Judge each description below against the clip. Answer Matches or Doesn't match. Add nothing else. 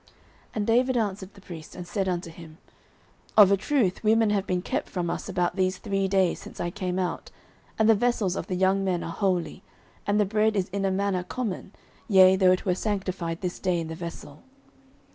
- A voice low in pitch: Doesn't match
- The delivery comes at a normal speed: Doesn't match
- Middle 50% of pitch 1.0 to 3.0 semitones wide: Matches